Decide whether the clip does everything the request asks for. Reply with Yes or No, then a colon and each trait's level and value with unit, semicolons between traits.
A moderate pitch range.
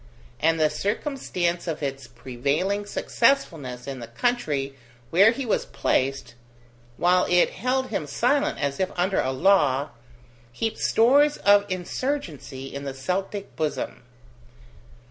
No: wide, 7.1 semitones